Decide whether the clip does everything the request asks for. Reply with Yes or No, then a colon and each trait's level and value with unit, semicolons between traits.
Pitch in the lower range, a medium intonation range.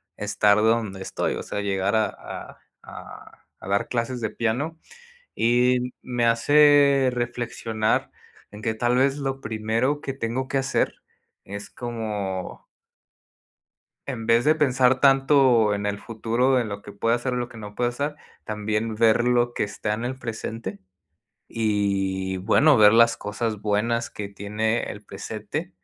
Yes: low, 115 Hz; average, 3.2 semitones